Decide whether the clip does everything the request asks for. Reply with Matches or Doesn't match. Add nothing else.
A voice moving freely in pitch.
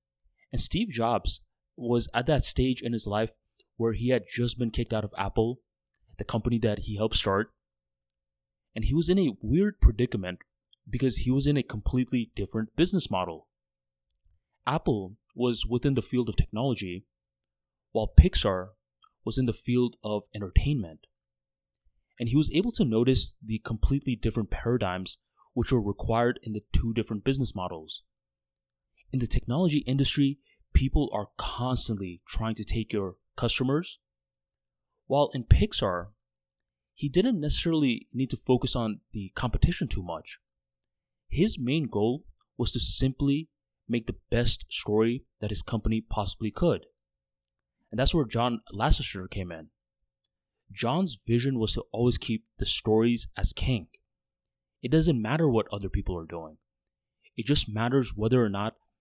Matches